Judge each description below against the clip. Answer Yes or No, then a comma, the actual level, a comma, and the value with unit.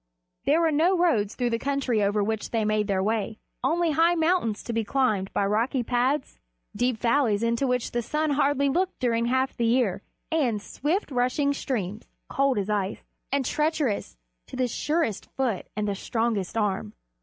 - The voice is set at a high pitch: Yes, high, 245 Hz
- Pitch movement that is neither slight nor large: Yes, average, 4.9 semitones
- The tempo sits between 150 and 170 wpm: No, average, 180 wpm